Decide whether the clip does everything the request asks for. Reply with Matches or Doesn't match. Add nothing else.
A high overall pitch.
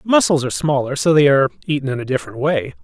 Doesn't match